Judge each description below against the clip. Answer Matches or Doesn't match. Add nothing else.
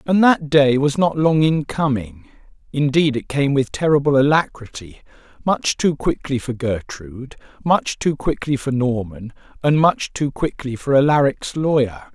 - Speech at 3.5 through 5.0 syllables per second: Matches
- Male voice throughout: Matches